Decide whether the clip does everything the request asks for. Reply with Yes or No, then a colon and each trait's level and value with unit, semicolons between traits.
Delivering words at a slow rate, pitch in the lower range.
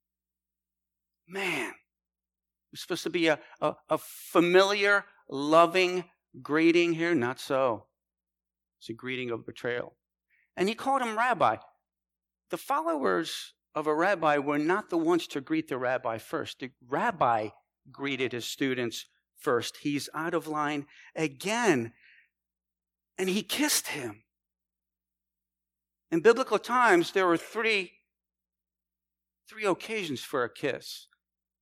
Yes: slow, 125 wpm; low, 130 Hz